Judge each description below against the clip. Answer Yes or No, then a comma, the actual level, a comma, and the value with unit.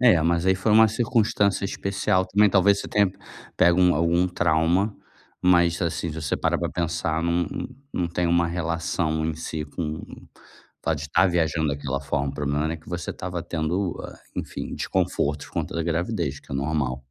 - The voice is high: No, very low, 85 Hz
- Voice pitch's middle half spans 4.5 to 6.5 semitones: No, average, 2.7 semitones